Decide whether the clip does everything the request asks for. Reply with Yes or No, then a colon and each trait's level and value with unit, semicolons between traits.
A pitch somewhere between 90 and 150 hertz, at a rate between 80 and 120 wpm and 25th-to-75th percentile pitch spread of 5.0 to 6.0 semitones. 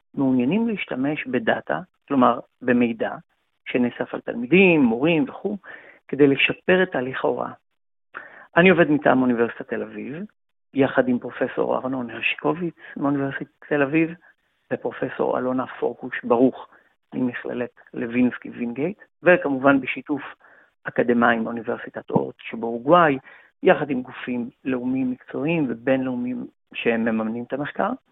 Yes: low, 135 Hz; average, 115 wpm; wide, 5.5 semitones